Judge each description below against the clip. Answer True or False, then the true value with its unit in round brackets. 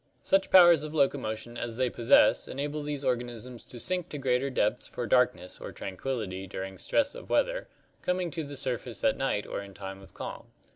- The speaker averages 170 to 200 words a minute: True (195 wpm)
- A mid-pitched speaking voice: False (125 Hz)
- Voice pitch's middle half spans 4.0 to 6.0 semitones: True (5.2 semitones)